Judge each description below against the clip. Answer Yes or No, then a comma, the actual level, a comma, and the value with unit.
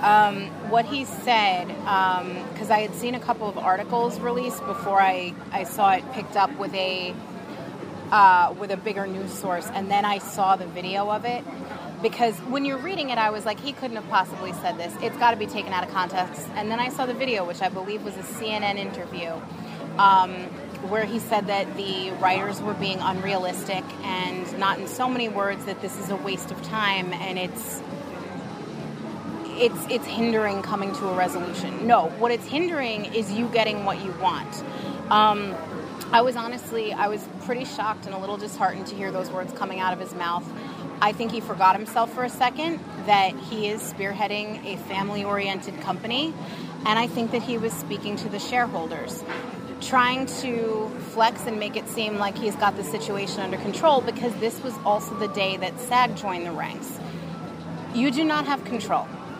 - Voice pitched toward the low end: No, high, 210 Hz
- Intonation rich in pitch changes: No, average, 3.4 semitones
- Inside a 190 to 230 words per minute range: Yes, average, 195 wpm